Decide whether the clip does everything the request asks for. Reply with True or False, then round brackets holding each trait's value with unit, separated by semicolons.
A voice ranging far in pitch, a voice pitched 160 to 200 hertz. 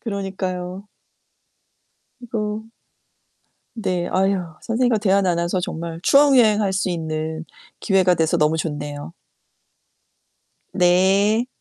False (3.7 semitones; 190 Hz)